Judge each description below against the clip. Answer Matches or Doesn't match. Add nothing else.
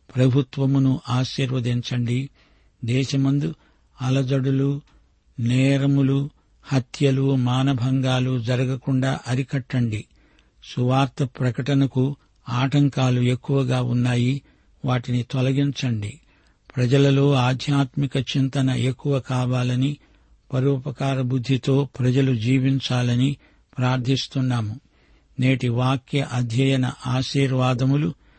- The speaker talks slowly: Matches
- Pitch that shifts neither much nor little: Doesn't match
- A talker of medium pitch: Doesn't match